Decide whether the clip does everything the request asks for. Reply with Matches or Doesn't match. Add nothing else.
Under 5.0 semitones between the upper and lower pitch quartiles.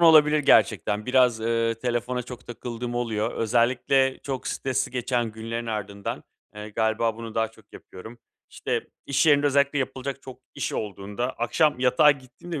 Matches